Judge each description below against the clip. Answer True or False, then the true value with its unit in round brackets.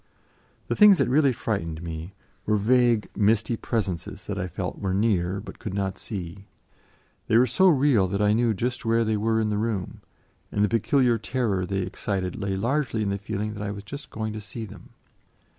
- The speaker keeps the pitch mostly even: False (3.0 semitones)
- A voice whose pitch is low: True (105 Hz)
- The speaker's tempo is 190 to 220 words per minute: True (200 wpm)